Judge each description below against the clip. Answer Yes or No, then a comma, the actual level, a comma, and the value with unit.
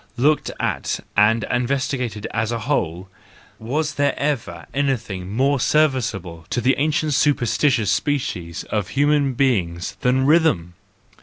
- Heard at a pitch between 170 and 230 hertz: No, low, 125 Hz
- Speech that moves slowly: Yes, slow, 125 wpm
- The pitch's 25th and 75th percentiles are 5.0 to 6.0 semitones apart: Yes, wide, 5.4 semitones